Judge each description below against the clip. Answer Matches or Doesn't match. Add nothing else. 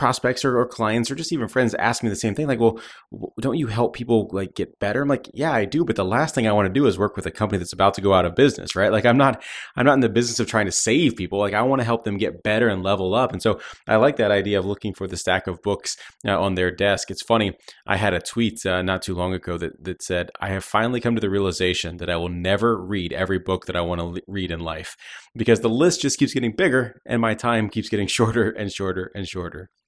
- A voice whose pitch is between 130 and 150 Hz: Doesn't match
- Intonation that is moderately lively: Matches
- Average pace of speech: Doesn't match